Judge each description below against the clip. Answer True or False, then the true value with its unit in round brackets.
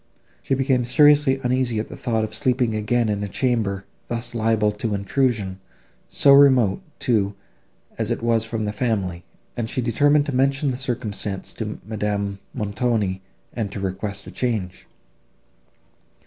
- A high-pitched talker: False (115 Hz)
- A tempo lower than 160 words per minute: True (150 wpm)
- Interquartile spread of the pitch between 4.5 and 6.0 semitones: False (3.7 semitones)